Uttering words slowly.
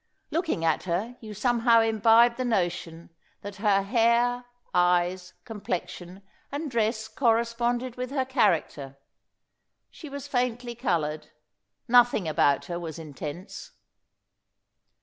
Yes: slow, 110 wpm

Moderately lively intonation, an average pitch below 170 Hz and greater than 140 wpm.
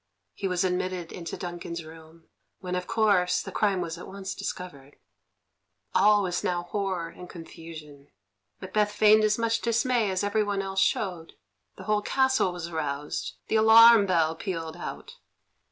No: average, 3.9 semitones; medium, 185 Hz; average, 155 wpm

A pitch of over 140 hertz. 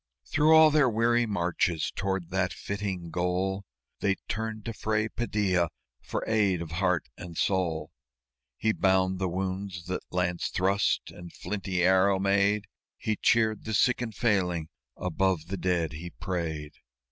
No: very low, 95 Hz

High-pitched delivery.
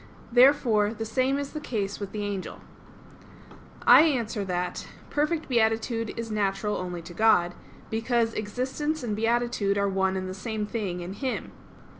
Yes: high, 220 Hz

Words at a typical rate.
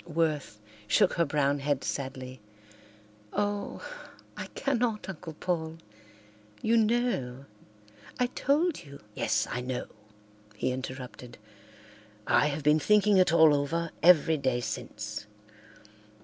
No: slow, 110 wpm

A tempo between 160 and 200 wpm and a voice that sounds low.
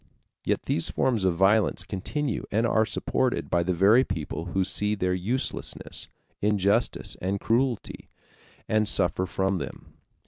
No: average, 140 wpm; low, 100 Hz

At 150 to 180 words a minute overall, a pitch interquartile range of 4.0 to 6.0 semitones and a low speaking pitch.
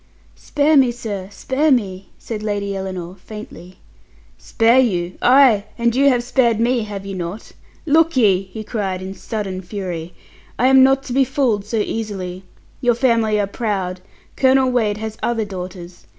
No: average, 160 wpm; average, 4.5 semitones; high, 215 Hz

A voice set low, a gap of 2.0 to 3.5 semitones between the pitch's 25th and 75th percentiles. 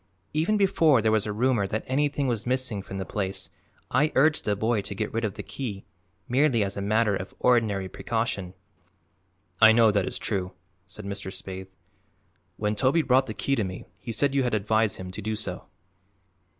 No: low, 110 Hz; average, 4.4 semitones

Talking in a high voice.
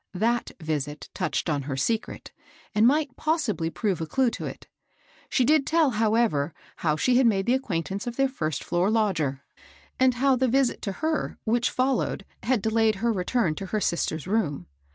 Yes: high, 220 Hz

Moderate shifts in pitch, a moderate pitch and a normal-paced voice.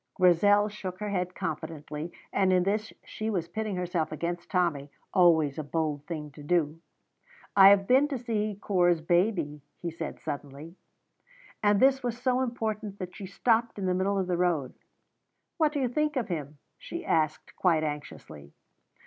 Yes: average, 4.8 semitones; medium, 180 Hz; average, 170 wpm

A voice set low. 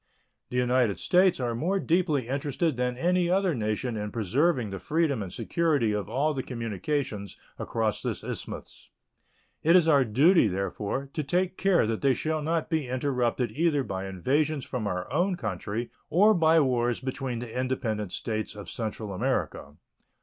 Yes: low, 130 Hz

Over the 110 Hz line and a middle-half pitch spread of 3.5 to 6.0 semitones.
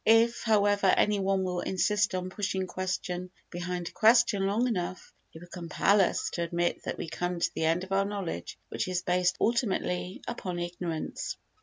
No: medium, 185 Hz; narrow, 2.4 semitones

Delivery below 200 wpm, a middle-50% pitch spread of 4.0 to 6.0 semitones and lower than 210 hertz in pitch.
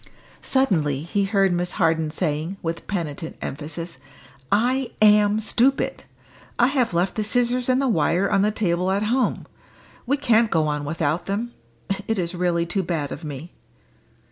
Yes: average, 160 wpm; average, 5.2 semitones; high, 190 Hz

